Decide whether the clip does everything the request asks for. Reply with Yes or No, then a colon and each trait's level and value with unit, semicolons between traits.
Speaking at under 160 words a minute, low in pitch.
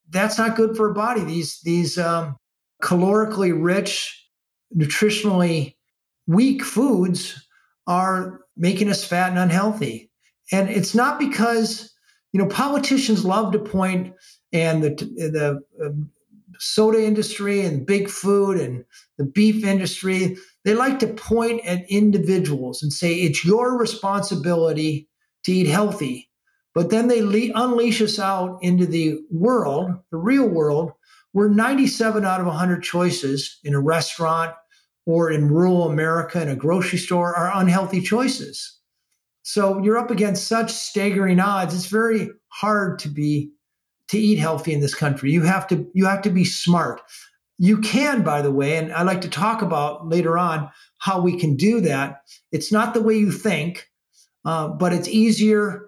No: average, 150 wpm; medium, 185 Hz